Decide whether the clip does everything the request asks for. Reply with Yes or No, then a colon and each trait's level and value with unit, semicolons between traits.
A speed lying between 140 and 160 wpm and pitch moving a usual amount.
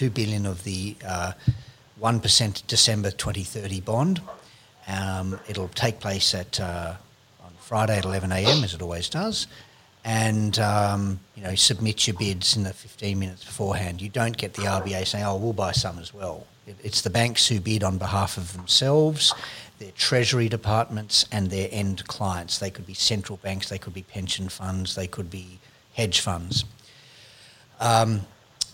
No: average, 170 wpm; average, 3.3 semitones